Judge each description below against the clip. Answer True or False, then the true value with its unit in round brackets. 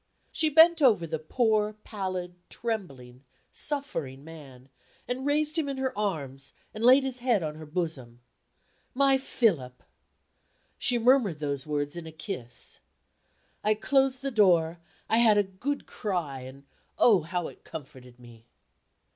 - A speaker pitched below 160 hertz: False (185 Hz)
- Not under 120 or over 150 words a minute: True (145 wpm)